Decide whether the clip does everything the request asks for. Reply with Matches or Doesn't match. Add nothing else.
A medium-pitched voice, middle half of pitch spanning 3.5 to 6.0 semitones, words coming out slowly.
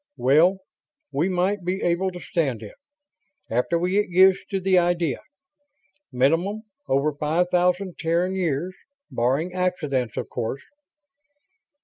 Matches